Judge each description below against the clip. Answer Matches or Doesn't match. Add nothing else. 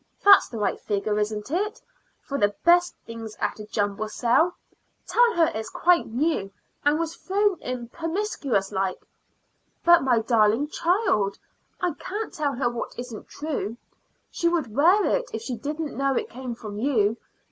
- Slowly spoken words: Doesn't match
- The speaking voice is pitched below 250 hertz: Doesn't match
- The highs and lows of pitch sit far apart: Matches